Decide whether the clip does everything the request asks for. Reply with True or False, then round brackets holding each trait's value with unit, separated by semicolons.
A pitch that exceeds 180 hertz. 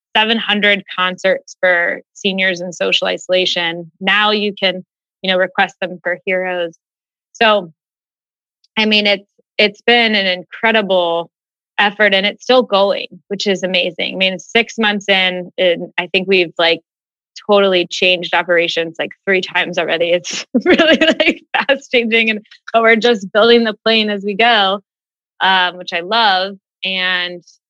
True (190 Hz)